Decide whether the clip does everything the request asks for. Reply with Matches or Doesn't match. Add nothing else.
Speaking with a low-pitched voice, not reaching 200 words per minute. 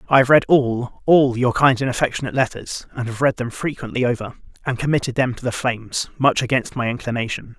Doesn't match